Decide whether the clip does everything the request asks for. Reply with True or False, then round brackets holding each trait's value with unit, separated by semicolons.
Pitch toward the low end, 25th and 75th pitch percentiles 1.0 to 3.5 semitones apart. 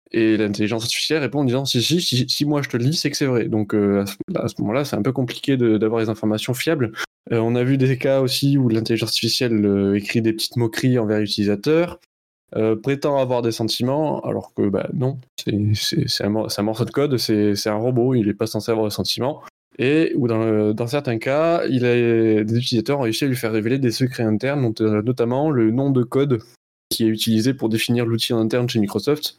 True (115 Hz; 3.2 semitones)